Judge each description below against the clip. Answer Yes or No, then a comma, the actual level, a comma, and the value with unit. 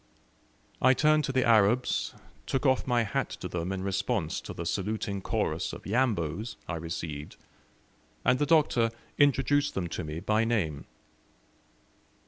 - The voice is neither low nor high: No, low, 110 Hz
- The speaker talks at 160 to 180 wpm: No, average, 145 wpm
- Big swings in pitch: Yes, wide, 6.4 semitones